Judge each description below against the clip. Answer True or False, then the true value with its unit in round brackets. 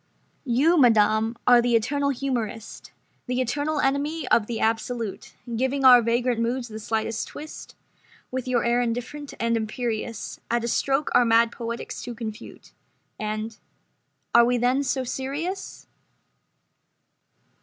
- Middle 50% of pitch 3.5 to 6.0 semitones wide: False (2.6 semitones)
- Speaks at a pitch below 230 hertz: False (240 Hz)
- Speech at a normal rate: False (130 wpm)